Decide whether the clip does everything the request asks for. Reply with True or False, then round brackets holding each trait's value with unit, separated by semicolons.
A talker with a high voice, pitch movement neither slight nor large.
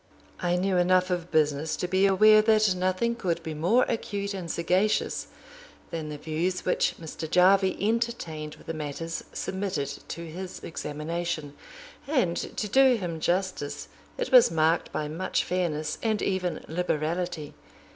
False (180 Hz; 3.5 semitones)